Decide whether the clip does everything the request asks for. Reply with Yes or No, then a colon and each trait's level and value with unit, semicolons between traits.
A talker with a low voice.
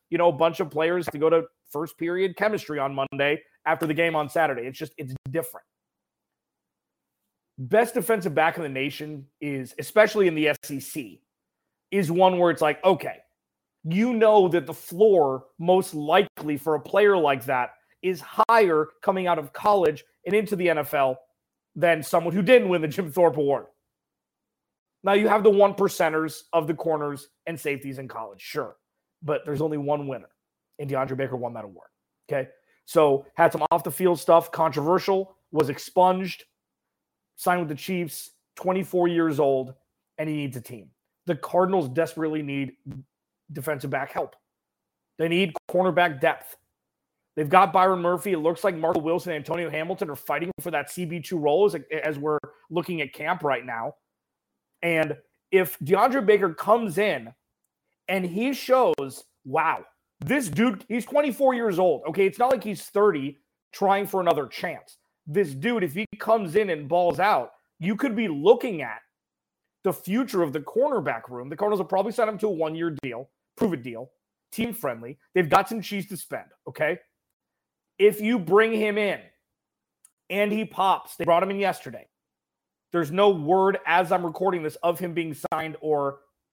No: medium, 170 Hz